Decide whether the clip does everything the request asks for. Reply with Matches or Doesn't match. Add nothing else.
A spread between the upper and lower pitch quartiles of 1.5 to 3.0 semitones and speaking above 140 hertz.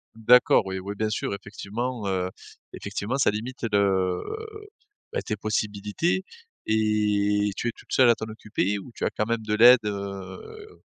Doesn't match